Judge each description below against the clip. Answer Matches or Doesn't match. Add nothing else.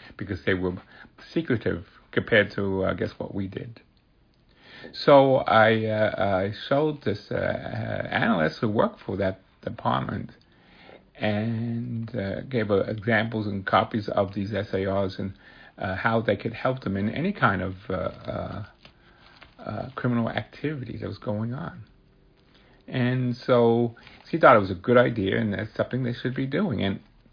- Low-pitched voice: Matches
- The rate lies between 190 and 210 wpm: Doesn't match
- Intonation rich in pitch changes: Doesn't match